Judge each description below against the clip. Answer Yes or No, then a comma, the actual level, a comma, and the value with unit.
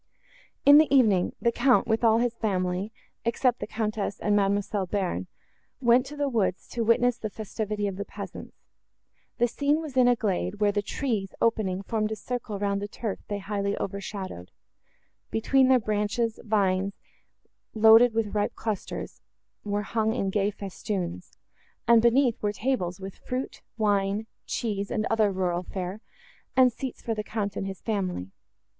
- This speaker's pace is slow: No, average, 160 wpm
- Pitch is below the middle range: No, high, 215 Hz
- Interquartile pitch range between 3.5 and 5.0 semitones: No, average, 2.9 semitones